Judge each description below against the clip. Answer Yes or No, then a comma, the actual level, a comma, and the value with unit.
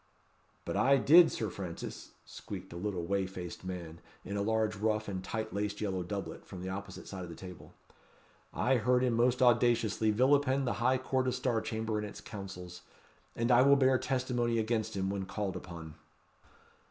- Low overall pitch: Yes, low, 110 Hz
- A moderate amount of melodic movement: Yes, average, 4.5 semitones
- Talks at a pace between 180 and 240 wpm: Yes, average, 185 wpm